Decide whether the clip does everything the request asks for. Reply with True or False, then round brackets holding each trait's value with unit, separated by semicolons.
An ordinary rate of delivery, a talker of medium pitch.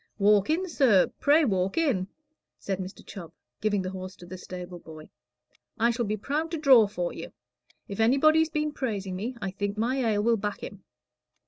False (190 wpm; 210 Hz)